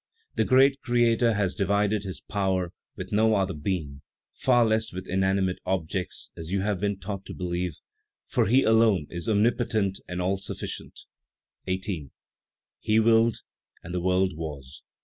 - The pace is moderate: Yes, average, 150 wpm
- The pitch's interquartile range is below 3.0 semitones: No, average, 3.4 semitones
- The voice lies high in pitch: No, very low, 95 Hz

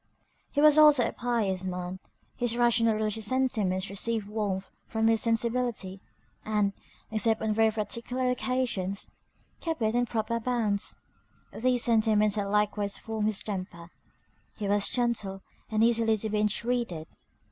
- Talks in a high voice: Yes, high, 220 Hz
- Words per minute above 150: No, average, 140 wpm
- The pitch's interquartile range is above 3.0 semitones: No, average, 2.7 semitones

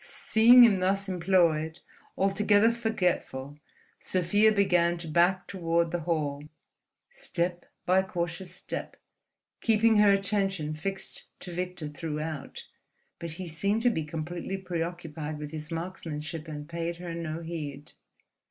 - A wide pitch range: No, average, 3.3 semitones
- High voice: No, medium, 175 Hz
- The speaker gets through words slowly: Yes, slow, 125 wpm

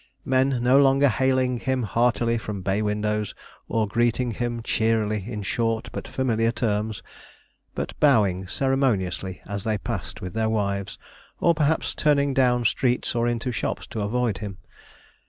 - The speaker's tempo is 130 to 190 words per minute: Yes, average, 150 wpm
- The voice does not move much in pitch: No, average, 3.5 semitones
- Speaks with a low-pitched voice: Yes, low, 115 Hz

